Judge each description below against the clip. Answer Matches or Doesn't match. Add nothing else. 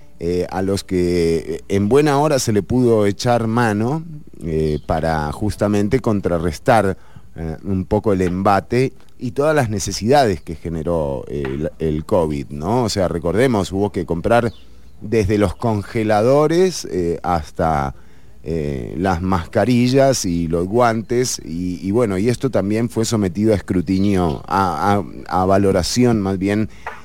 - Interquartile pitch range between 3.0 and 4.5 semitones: Doesn't match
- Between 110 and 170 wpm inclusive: Matches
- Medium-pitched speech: Doesn't match